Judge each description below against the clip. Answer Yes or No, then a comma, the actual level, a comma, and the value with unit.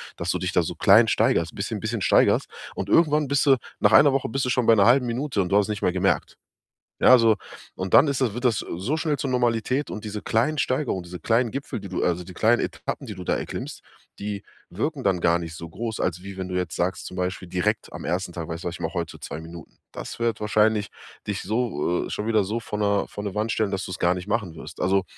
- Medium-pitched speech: No, low, 105 Hz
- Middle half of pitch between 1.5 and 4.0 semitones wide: No, average, 4.5 semitones